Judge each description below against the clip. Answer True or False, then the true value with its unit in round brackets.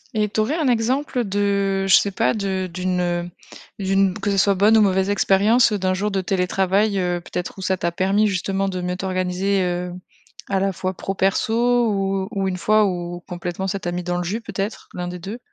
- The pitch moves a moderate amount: False (2.1 semitones)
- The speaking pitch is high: True (195 Hz)